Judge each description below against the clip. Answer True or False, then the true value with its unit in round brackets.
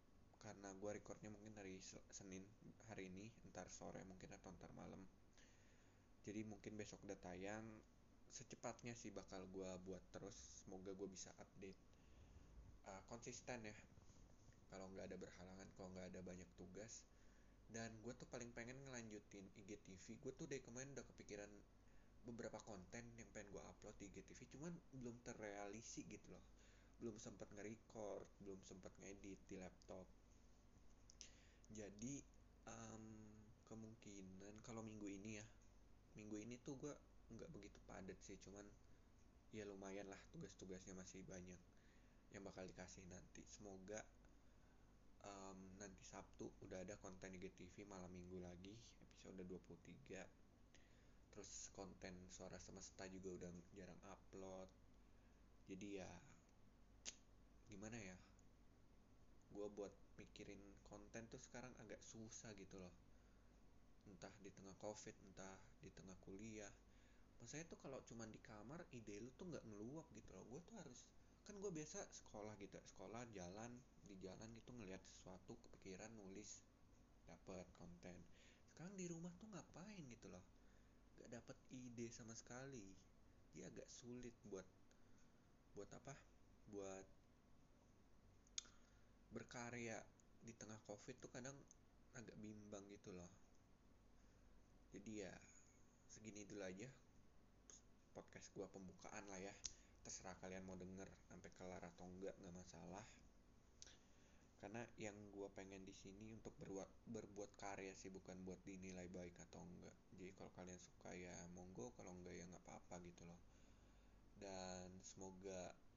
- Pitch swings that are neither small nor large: True (3.1 semitones)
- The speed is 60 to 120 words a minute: False (135 wpm)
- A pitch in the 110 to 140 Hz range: False (100 Hz)